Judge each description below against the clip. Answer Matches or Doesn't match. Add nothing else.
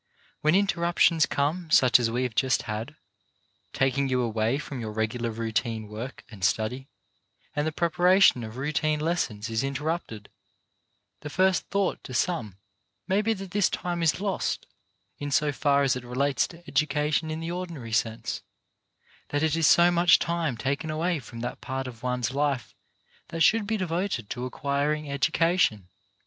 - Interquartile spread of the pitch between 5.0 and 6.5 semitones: Matches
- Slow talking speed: Doesn't match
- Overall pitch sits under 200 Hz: Matches